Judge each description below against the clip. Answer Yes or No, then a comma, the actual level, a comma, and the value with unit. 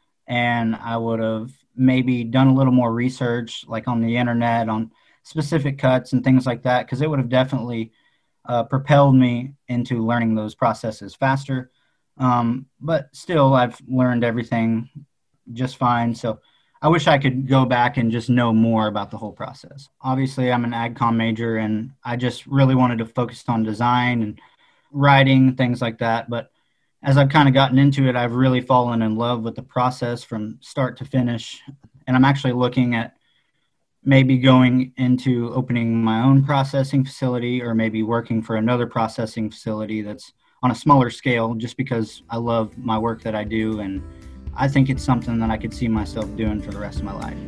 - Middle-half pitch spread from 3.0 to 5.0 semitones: No, narrow, 2.4 semitones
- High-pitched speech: No, low, 120 Hz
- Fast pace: No, average, 185 wpm